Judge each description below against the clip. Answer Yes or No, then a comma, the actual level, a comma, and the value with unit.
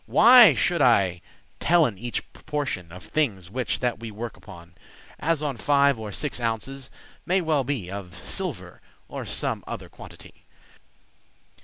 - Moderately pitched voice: No, low, 120 Hz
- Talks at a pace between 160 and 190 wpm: No, average, 145 wpm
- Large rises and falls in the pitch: Yes, wide, 6.7 semitones